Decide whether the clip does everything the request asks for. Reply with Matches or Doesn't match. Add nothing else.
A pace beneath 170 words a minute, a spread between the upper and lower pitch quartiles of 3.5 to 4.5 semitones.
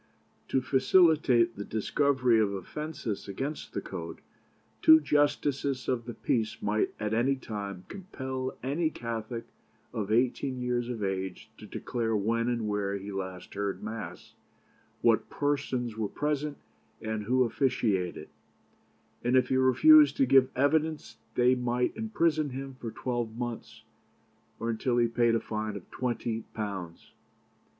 Matches